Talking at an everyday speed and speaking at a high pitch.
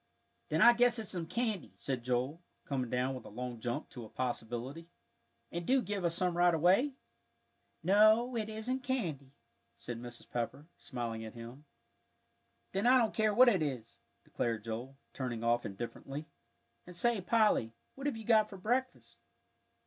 No: average, 165 wpm; medium, 165 Hz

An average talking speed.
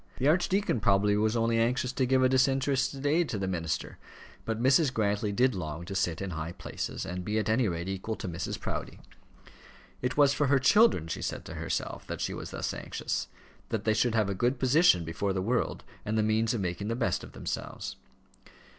No: fast, 210 wpm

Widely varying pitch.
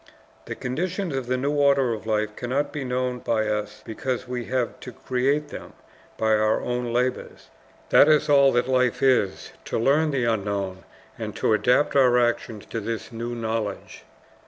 No: average, 3.4 semitones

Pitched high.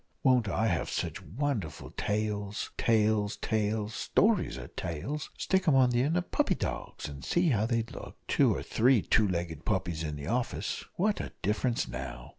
No: low, 110 Hz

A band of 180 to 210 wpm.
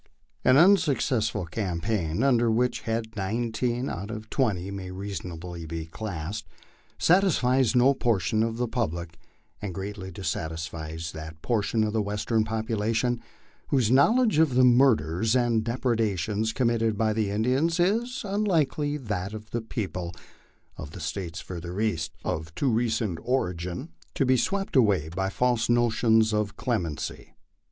No: average, 140 wpm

